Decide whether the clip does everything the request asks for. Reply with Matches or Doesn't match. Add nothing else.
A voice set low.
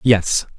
Matches